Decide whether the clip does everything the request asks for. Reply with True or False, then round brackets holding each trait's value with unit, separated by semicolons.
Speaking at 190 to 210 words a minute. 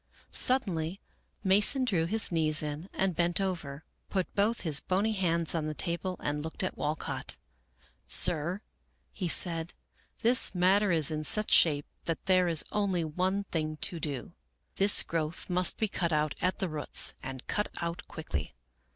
False (170 wpm)